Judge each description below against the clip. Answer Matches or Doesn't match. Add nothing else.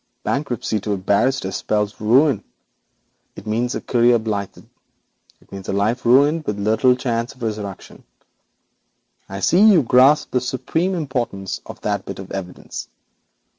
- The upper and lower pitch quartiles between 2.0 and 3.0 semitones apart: Doesn't match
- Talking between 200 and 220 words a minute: Doesn't match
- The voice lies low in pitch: Matches